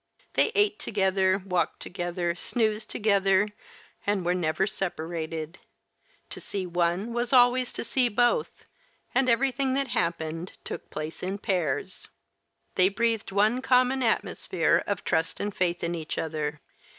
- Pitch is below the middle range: No, high, 195 Hz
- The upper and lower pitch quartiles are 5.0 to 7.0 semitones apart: Yes, wide, 5.4 semitones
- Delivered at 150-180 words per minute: No, average, 140 wpm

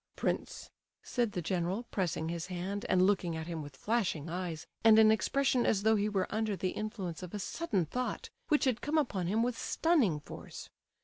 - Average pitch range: Yes, average, 4.5 semitones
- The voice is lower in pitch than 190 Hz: No, high, 200 Hz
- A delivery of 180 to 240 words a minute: Yes, average, 195 wpm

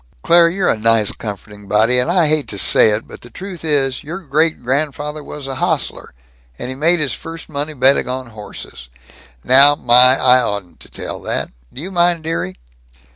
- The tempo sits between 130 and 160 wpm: No, average, 185 wpm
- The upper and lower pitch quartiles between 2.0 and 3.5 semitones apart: No, average, 4.9 semitones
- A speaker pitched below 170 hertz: Yes, low, 135 Hz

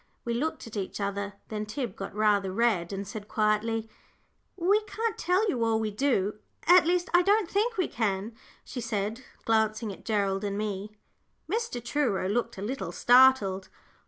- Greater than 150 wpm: Yes, average, 170 wpm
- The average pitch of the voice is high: Yes, high, 220 Hz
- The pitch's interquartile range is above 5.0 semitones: Yes, wide, 5.4 semitones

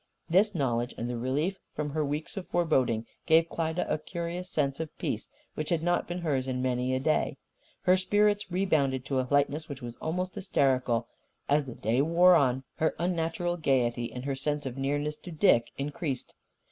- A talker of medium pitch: Yes, medium, 150 Hz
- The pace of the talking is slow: No, average, 185 wpm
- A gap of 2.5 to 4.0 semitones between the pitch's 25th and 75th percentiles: No, average, 4.8 semitones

